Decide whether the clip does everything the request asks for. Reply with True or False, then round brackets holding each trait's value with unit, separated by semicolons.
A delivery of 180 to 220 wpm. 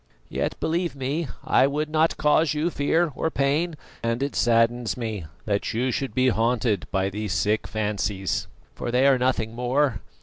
False (170 wpm)